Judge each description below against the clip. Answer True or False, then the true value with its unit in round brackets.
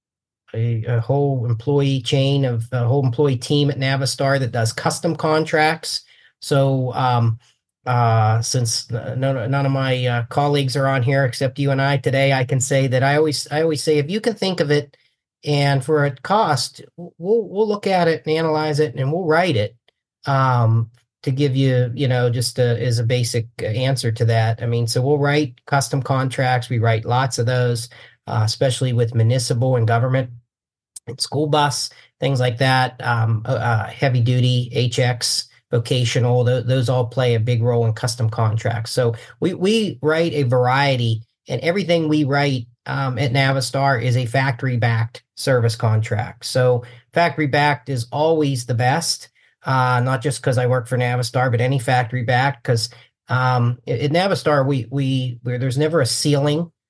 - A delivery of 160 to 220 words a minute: True (180 wpm)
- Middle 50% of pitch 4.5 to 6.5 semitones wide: False (2.8 semitones)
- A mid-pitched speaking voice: False (130 Hz)